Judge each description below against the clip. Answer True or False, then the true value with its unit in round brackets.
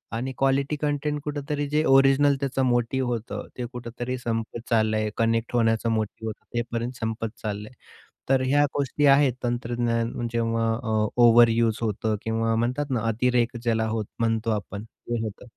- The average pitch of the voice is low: True (120 Hz)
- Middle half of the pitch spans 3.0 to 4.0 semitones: False (2.6 semitones)